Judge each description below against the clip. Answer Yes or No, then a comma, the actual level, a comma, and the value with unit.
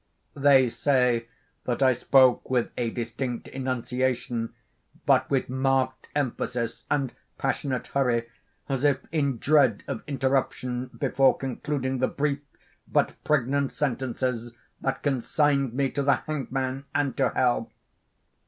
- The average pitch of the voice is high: No, low, 130 Hz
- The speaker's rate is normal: No, slow, 125 wpm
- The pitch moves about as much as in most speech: No, narrow, 1.9 semitones